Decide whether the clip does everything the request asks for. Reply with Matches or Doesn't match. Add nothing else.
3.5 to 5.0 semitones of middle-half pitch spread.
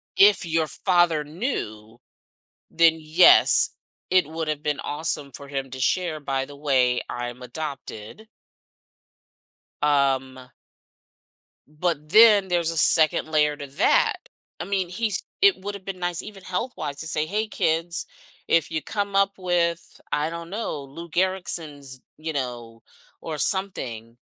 Matches